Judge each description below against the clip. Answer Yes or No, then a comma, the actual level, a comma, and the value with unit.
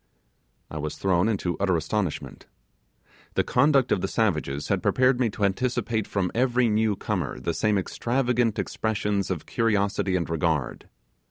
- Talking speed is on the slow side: No, average, 145 wpm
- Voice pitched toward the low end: Yes, low, 100 Hz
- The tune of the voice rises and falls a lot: No, average, 4.6 semitones